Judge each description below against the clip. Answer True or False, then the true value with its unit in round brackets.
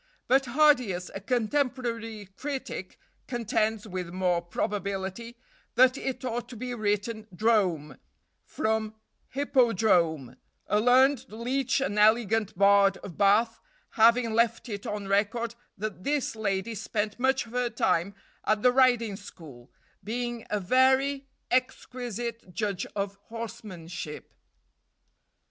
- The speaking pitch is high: True (220 Hz)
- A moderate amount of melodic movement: True (3.7 semitones)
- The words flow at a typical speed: False (120 wpm)